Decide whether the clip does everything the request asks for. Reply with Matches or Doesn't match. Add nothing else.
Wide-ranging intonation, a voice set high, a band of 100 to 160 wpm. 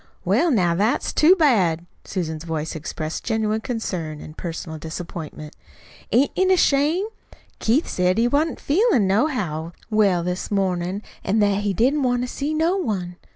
Matches